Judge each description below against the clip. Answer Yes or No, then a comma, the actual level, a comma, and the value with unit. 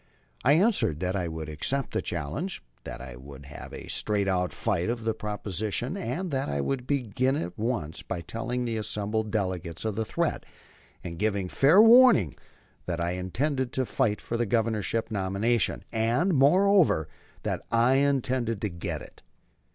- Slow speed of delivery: No, average, 170 wpm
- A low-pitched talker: Yes, low, 110 Hz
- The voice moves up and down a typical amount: No, wide, 6.3 semitones